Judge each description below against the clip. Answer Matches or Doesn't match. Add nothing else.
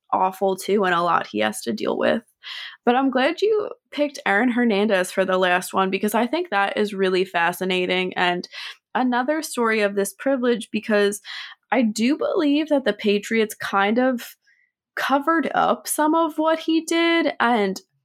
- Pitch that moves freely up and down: Matches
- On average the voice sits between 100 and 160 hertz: Doesn't match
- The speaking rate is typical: Matches